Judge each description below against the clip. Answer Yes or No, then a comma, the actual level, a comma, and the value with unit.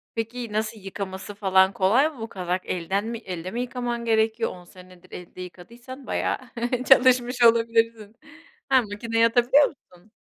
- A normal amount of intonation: Yes, average, 4.1 semitones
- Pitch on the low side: No, high, 225 Hz